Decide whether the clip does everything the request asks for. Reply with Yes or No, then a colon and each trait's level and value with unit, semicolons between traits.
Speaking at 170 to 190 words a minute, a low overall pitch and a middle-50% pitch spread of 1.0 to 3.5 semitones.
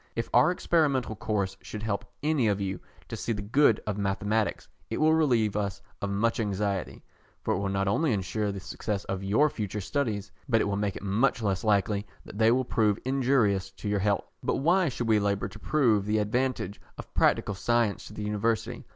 No: fast, 205 wpm; low, 105 Hz; average, 3.0 semitones